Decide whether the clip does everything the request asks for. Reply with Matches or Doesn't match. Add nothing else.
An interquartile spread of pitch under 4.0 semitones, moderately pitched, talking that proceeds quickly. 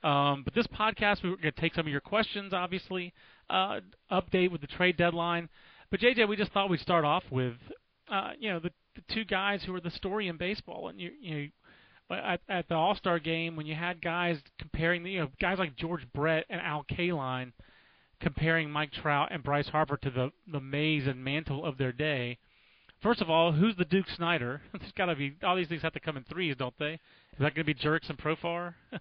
Matches